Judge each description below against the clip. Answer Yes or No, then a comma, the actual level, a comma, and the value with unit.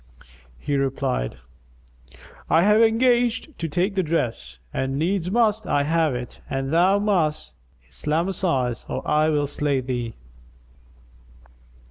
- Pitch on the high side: No, medium, 155 Hz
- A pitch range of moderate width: No, wide, 6.4 semitones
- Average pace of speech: No, slow, 120 wpm